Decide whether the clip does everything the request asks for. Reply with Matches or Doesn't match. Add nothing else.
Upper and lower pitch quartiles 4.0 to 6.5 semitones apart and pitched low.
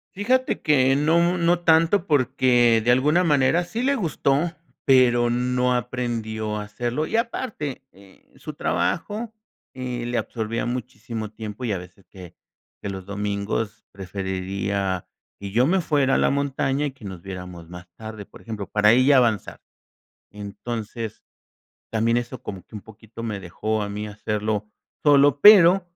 Matches